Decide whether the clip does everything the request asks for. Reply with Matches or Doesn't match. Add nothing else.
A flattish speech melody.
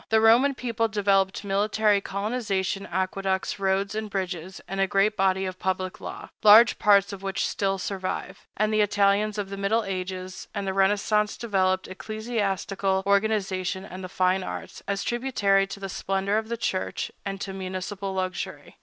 Matches